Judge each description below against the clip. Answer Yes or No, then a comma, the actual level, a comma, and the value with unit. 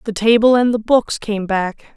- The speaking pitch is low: No, high, 220 Hz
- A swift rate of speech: Yes, fast, 215 wpm